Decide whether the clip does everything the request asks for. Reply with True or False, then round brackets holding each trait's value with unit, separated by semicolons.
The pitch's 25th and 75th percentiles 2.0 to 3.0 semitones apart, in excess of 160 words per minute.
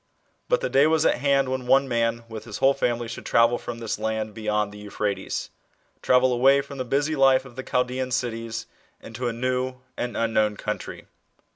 True (2.7 semitones; 190 wpm)